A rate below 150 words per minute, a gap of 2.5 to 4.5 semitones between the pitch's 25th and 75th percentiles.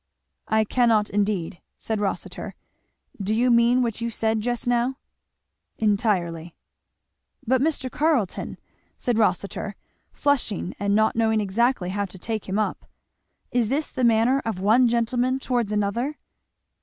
Yes: slow, 135 wpm; average, 3.1 semitones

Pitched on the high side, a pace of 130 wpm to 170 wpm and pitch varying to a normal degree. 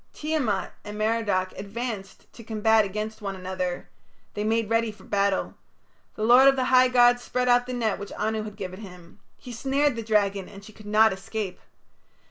No: high, 215 Hz; average, 185 wpm; average, 3.3 semitones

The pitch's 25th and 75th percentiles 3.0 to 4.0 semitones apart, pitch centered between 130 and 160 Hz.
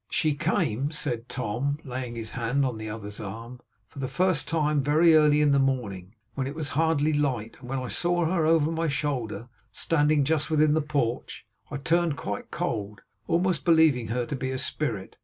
No: average, 4.5 semitones; medium, 140 Hz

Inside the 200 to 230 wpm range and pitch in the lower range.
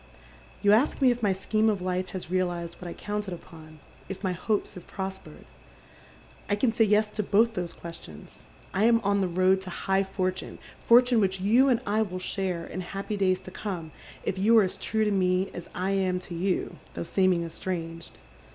No: fast, 205 wpm; high, 190 Hz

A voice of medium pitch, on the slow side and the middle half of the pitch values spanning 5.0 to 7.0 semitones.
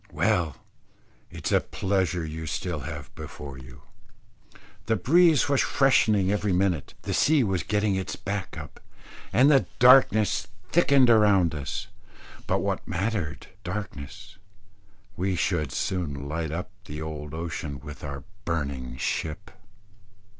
No: very low, 90 Hz; slow, 125 wpm; wide, 5.4 semitones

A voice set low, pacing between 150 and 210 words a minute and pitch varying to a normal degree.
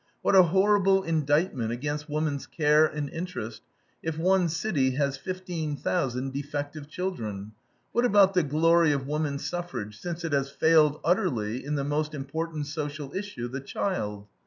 No: medium, 150 Hz; average, 155 wpm; average, 3.9 semitones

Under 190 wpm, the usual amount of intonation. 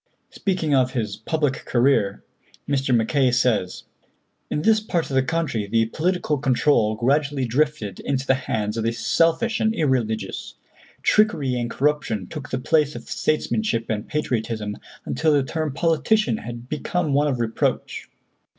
Yes: average, 150 wpm; average, 4.9 semitones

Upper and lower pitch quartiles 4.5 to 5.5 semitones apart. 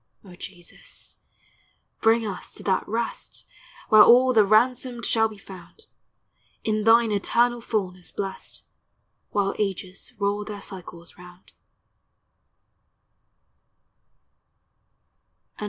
No: average, 3.2 semitones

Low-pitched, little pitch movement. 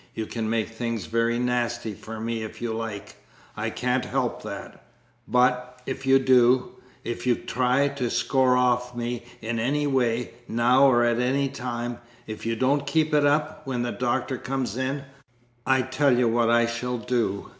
Yes: low, 125 Hz; narrow, 2.0 semitones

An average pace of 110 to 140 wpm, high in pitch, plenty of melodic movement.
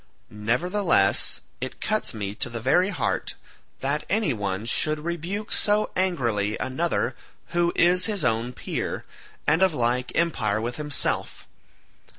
No: slow, 135 wpm; medium, 150 Hz; wide, 7.5 semitones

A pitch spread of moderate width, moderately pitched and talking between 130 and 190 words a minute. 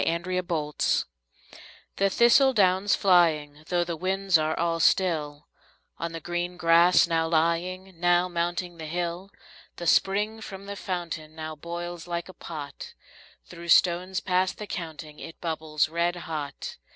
No: narrow, 2.2 semitones; medium, 175 Hz; average, 140 wpm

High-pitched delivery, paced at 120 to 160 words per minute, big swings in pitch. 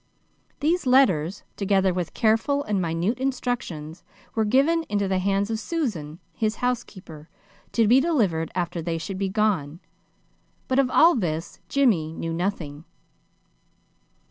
Yes: high, 200 Hz; slow, 135 wpm; wide, 6.9 semitones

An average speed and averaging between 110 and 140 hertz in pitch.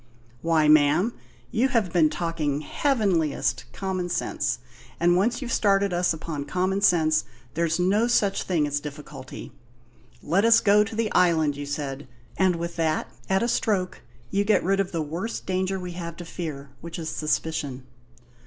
No: average, 170 wpm; medium, 175 Hz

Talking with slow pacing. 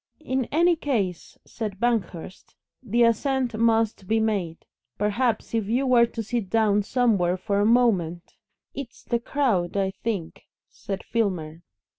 No: average, 145 wpm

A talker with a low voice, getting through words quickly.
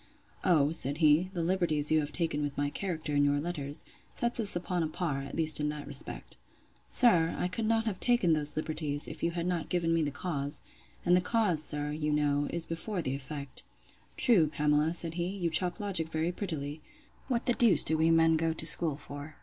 No: medium, 160 Hz; fast, 215 wpm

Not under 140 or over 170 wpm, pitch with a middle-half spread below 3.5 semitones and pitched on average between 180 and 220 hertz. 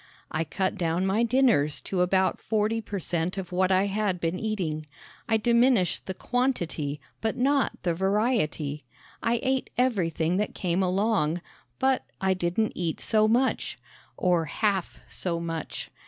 No: average, 150 wpm; average, 4.7 semitones; high, 190 Hz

